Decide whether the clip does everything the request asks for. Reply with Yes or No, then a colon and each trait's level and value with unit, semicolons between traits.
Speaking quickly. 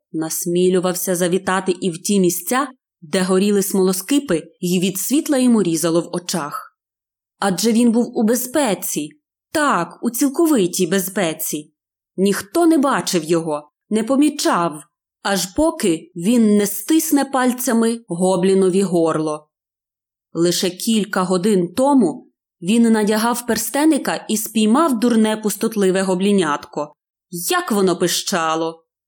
No: average, 110 wpm